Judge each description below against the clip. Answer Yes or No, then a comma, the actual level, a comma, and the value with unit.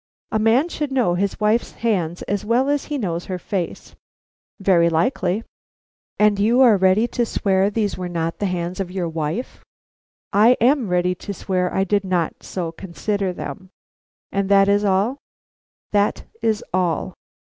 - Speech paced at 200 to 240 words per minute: No, average, 165 wpm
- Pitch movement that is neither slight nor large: Yes, average, 3.4 semitones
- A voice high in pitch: Yes, high, 195 Hz